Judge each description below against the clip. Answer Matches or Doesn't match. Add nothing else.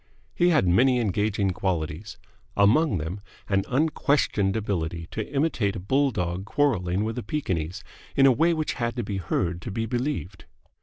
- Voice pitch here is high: Doesn't match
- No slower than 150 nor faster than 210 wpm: Matches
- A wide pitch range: Matches